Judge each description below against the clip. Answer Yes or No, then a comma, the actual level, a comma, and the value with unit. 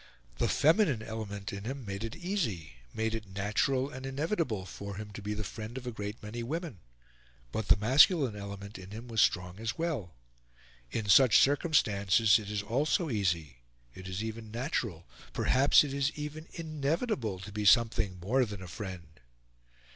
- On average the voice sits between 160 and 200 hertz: No, low, 110 Hz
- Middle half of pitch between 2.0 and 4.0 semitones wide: No, average, 5.2 semitones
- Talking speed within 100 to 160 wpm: No, average, 170 wpm